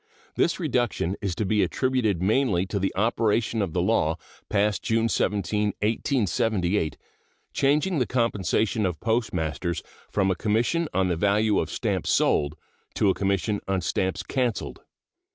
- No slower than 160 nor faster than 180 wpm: No, average, 145 wpm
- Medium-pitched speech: No, low, 105 Hz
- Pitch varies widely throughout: No, average, 3.3 semitones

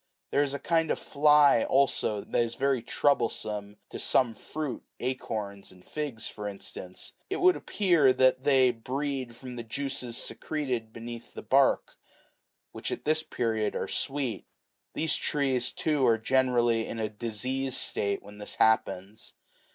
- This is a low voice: Yes, low, 125 Hz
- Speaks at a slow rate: No, average, 150 wpm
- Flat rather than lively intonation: No, average, 4.0 semitones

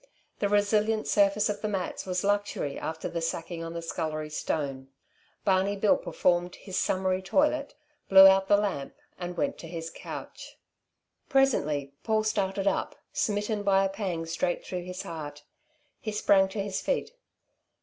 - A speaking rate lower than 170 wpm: Yes, average, 160 wpm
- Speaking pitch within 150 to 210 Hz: Yes, high, 190 Hz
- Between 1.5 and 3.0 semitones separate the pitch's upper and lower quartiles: No, average, 3.6 semitones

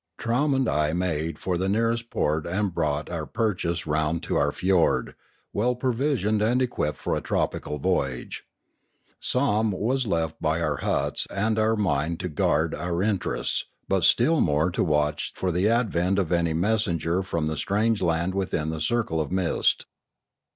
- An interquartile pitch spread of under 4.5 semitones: No, wide, 5.6 semitones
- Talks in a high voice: No, very low, 90 Hz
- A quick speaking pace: No, average, 165 wpm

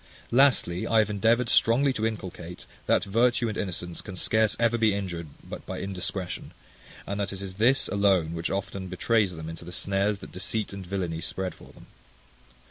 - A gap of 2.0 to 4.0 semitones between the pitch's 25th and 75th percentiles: Yes, average, 3.6 semitones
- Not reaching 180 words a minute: No, average, 185 wpm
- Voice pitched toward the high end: No, low, 100 Hz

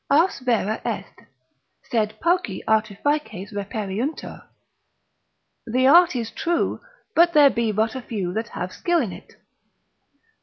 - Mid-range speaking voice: No, high, 230 Hz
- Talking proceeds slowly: Yes, slow, 125 wpm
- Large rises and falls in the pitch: Yes, wide, 5.8 semitones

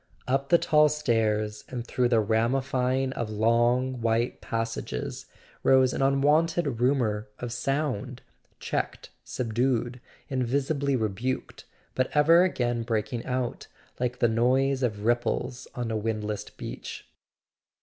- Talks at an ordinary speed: No, slow, 120 wpm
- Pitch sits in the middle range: No, low, 125 Hz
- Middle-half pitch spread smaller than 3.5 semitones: Yes, average, 2.8 semitones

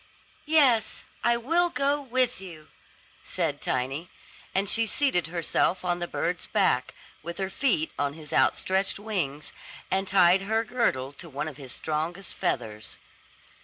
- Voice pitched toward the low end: No, medium, 180 Hz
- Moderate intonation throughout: No, wide, 6.6 semitones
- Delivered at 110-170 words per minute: Yes, average, 145 wpm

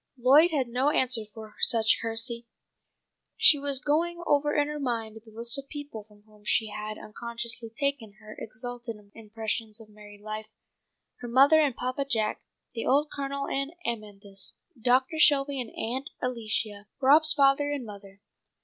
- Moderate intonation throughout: Yes, average, 4.3 semitones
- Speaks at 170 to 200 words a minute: No, average, 160 wpm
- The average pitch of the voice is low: No, high, 235 Hz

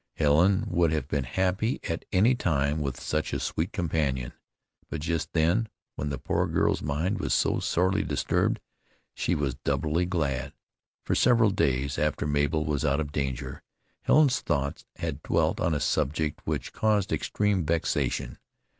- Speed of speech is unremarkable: Yes, average, 155 wpm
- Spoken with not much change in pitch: No, average, 4.2 semitones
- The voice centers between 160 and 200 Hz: No, very low, 80 Hz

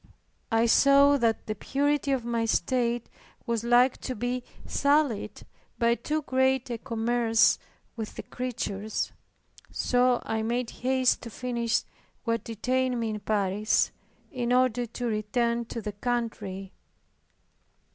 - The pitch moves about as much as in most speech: No, narrow, 2.2 semitones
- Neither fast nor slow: No, slow, 130 wpm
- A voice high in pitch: Yes, high, 235 Hz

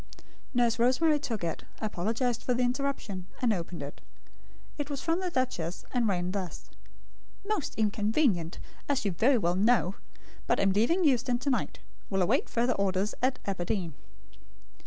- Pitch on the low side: No, high, 230 Hz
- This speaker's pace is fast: No, average, 155 wpm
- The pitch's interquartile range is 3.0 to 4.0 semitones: No, wide, 5.5 semitones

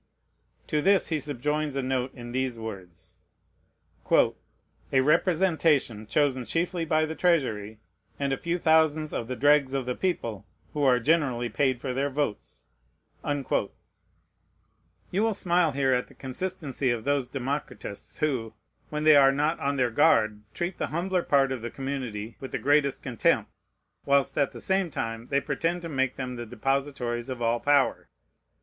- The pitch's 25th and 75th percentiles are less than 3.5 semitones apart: No, average, 3.8 semitones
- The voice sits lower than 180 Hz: Yes, medium, 140 Hz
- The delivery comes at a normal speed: Yes, average, 160 wpm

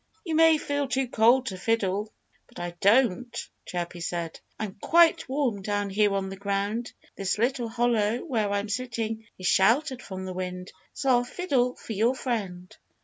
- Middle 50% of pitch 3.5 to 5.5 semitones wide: Yes, average, 4.5 semitones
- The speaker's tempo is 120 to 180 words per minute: Yes, average, 170 wpm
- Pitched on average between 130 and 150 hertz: No, high, 220 Hz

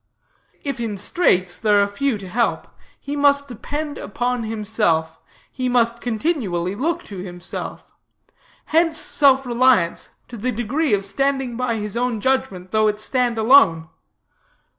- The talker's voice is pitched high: Yes, high, 235 Hz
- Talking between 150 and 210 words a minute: No, average, 140 wpm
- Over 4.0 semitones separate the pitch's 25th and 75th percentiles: Yes, average, 4.9 semitones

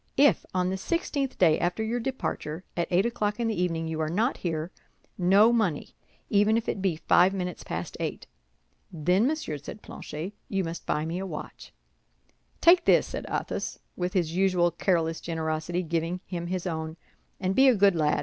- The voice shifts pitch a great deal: No, average, 4.0 semitones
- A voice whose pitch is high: No, medium, 180 Hz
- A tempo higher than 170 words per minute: Yes, average, 185 wpm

